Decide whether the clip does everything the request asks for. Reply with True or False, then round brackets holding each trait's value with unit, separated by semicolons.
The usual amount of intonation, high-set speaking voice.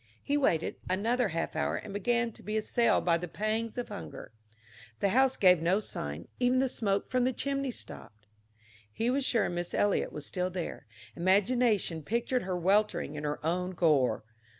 False (5.9 semitones; 200 Hz)